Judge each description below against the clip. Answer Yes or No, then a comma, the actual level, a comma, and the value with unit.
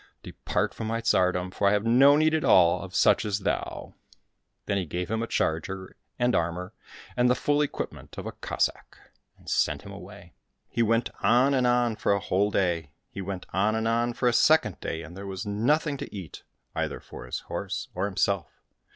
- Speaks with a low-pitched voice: Yes, low, 105 Hz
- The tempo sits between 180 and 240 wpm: Yes, fast, 205 wpm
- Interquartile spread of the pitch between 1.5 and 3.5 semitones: No, average, 4.7 semitones